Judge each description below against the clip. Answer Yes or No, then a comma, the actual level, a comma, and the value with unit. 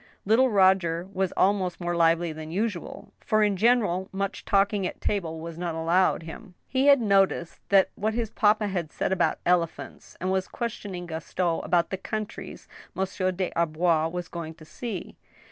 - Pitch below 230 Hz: Yes, medium, 185 Hz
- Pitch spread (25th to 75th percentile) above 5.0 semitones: No, average, 3.3 semitones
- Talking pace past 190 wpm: No, average, 165 wpm